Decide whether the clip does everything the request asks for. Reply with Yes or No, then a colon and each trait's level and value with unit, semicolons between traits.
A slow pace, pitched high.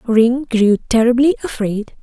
Yes: slow, 120 wpm; high, 235 Hz